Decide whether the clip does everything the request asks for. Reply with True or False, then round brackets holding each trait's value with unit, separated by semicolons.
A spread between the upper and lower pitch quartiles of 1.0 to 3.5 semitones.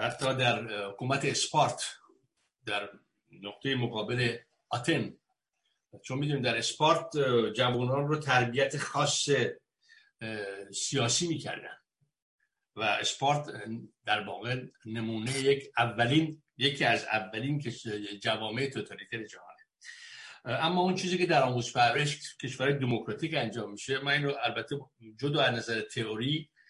False (4.1 semitones)